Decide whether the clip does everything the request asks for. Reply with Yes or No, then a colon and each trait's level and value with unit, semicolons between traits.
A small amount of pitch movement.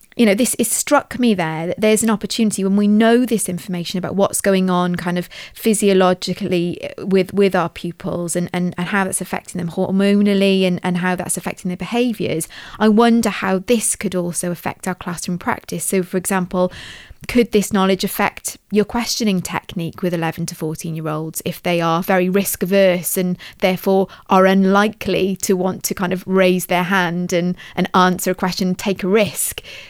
Yes: narrow, 2.1 semitones